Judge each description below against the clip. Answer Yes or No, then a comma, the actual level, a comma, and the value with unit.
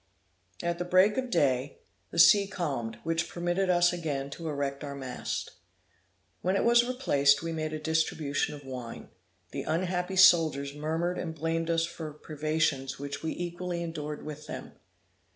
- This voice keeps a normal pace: Yes, average, 155 wpm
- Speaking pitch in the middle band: Yes, medium, 160 Hz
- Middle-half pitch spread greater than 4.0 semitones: No, average, 3.6 semitones